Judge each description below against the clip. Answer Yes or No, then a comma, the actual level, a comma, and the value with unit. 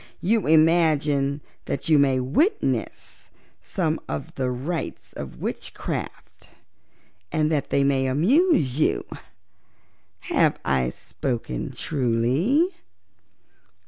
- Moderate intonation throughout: Yes, average, 4.1 semitones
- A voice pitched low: No, medium, 145 Hz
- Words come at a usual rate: No, slow, 95 wpm